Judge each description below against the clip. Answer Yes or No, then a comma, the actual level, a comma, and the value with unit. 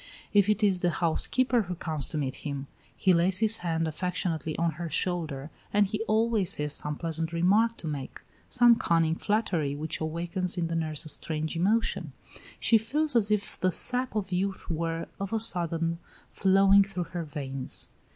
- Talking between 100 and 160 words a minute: No, average, 180 wpm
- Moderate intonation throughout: Yes, average, 4.2 semitones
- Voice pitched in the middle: Yes, medium, 175 Hz